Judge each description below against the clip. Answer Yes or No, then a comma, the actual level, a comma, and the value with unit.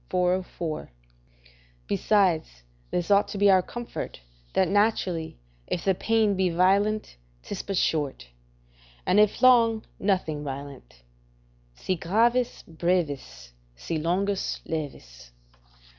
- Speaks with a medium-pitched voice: Yes, medium, 180 Hz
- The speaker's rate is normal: No, slow, 110 wpm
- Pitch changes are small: No, average, 4.7 semitones